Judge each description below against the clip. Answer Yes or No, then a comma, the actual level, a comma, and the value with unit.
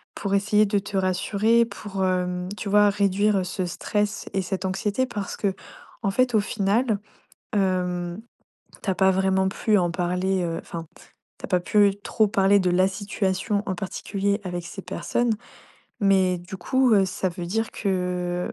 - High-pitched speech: Yes, high, 195 Hz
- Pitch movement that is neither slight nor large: No, narrow, 2.2 semitones